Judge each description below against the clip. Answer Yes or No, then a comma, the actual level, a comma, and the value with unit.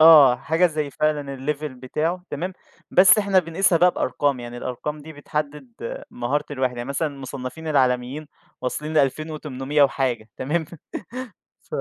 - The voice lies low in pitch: No, medium, 145 Hz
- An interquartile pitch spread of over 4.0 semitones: No, average, 3.5 semitones